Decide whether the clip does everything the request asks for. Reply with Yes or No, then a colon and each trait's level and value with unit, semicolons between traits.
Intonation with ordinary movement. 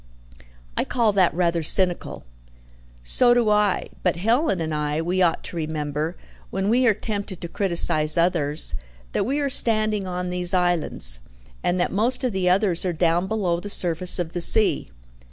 Yes: average, 3.8 semitones